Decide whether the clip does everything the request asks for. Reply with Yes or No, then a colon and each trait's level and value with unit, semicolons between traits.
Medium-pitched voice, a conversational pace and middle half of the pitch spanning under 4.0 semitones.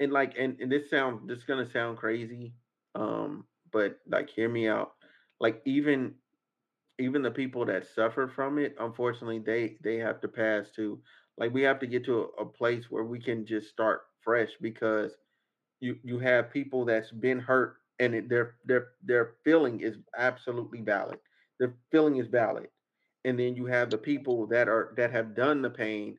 No: low, 120 Hz; average, 190 wpm; narrow, 2.4 semitones